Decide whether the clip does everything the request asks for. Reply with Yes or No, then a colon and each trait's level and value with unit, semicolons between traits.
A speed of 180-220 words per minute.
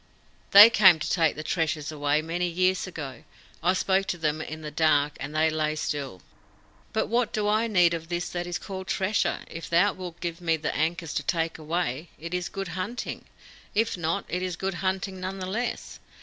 Yes: fast, 205 wpm